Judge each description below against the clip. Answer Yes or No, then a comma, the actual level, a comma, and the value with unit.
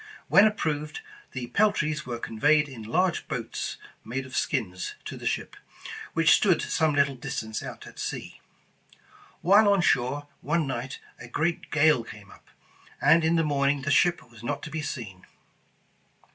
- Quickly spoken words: No, average, 165 wpm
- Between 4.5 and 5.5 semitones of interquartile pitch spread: Yes, average, 4.9 semitones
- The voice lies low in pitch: No, medium, 145 Hz